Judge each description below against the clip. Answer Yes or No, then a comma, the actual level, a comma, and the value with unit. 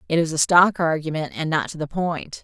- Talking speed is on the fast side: Yes, fast, 245 wpm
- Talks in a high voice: No, medium, 160 Hz